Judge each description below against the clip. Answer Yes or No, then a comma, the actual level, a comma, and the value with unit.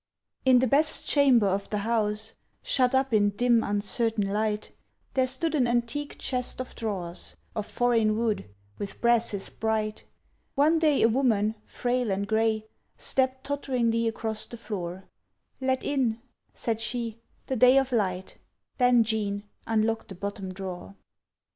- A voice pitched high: Yes, high, 225 Hz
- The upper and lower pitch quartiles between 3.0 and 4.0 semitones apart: Yes, average, 3.3 semitones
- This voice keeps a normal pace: Yes, average, 145 wpm